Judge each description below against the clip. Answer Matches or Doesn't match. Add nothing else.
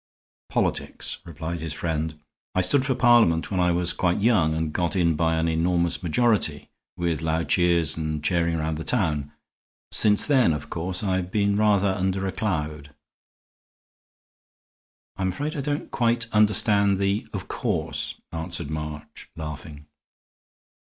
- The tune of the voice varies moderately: Matches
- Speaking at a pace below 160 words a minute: Matches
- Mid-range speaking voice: Doesn't match